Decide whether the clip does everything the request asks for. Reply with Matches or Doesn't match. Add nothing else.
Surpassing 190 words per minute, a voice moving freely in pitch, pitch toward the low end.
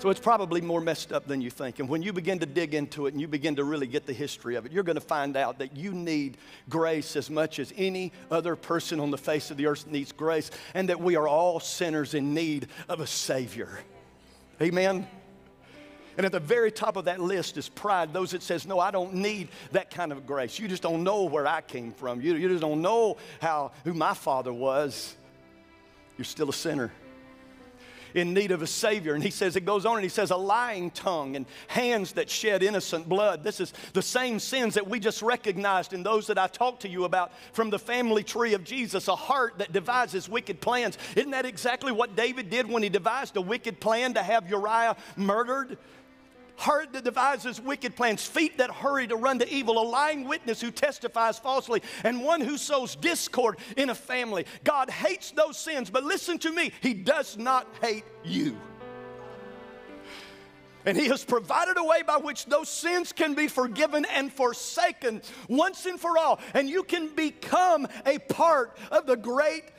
Doesn't match